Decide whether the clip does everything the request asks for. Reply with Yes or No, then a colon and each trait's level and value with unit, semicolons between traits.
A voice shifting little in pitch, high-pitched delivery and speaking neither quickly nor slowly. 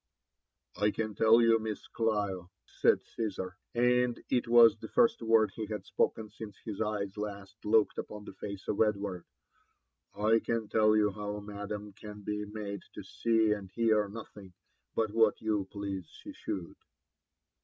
No: narrow, 1.7 semitones; low, 105 Hz; average, 165 wpm